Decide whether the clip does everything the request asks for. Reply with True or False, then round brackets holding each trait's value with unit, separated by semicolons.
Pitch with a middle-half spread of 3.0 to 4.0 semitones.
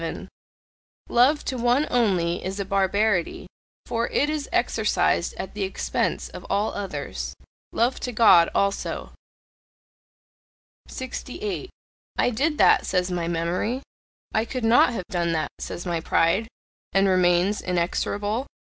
False (5.3 semitones)